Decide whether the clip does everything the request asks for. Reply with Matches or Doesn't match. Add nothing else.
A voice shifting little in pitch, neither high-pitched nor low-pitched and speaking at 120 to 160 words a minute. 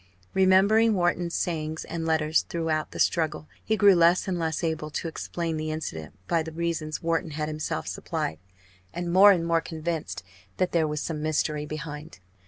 Doesn't match